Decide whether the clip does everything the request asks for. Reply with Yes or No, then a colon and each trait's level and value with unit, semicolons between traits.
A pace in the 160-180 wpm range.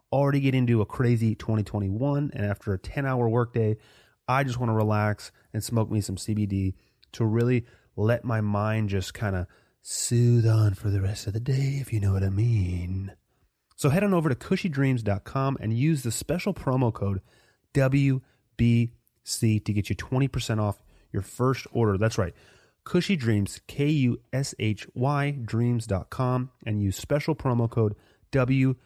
Yes: average, 165 wpm